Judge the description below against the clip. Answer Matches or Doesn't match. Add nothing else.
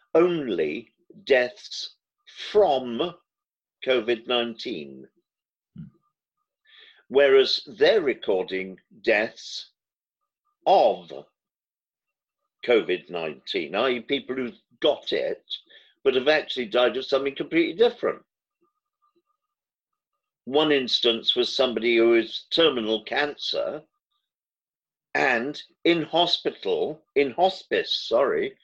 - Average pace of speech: Doesn't match